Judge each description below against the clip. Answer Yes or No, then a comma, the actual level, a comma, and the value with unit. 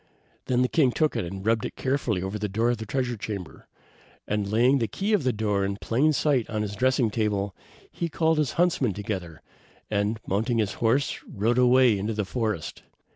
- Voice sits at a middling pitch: No, low, 110 Hz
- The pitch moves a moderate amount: Yes, average, 4.0 semitones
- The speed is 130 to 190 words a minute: No, average, 200 wpm